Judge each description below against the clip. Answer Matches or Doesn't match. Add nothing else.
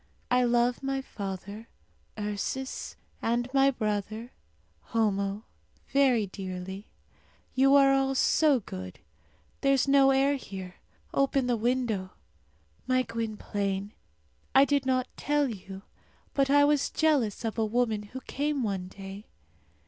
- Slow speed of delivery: Matches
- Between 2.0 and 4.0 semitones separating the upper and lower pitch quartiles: Doesn't match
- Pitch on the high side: Matches